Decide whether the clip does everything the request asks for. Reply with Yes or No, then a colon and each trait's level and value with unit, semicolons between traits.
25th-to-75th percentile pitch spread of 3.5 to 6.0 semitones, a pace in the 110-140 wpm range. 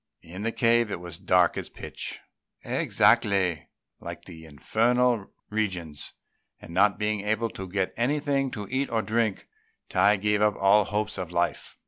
No: average, 3.8 semitones; average, 160 wpm